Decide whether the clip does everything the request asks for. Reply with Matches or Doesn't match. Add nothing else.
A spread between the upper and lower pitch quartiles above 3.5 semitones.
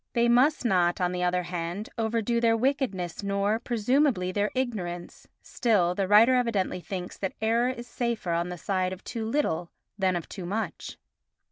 Matches